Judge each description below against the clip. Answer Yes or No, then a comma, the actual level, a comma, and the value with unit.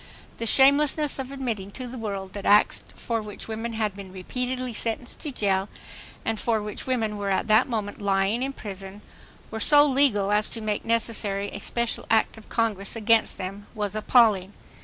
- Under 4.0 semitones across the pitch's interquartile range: Yes, average, 3.0 semitones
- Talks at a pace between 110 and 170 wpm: No, average, 180 wpm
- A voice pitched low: No, high, 220 Hz